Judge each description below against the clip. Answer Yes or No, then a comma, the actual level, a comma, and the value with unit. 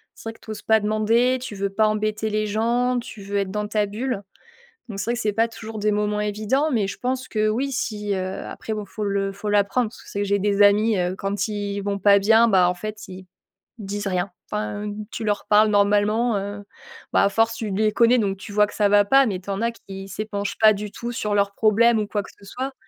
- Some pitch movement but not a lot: No, narrow, 1.7 semitones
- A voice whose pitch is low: No, high, 210 Hz